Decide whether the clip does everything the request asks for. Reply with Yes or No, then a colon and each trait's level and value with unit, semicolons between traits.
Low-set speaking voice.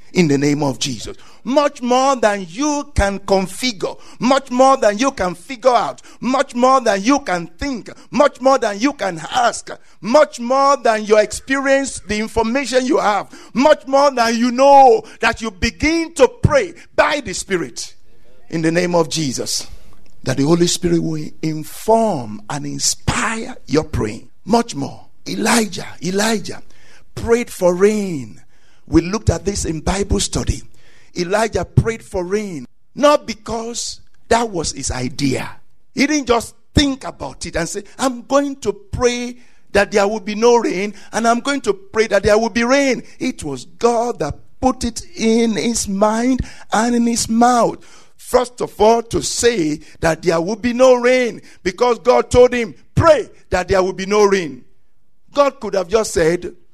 No: high, 225 Hz